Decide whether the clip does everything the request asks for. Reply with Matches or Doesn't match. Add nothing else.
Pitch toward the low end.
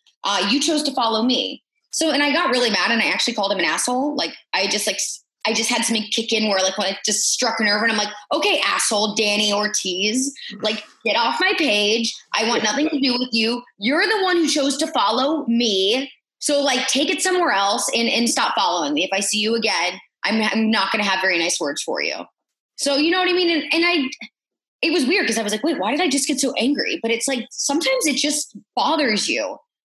Doesn't match